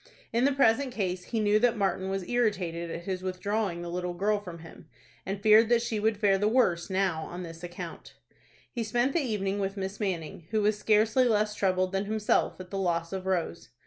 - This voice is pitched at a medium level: No, high, 195 Hz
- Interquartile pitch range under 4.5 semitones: Yes, average, 3.2 semitones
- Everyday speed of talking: No, fast, 210 wpm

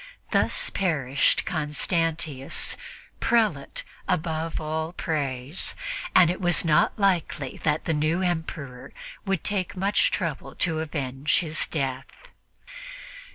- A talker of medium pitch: Yes, medium, 160 Hz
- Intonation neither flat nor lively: Yes, average, 3.5 semitones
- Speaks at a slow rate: Yes, slow, 110 wpm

